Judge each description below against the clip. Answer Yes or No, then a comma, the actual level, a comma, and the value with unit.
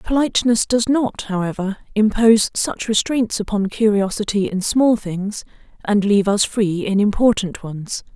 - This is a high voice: Yes, high, 210 Hz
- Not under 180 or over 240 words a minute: No, average, 140 wpm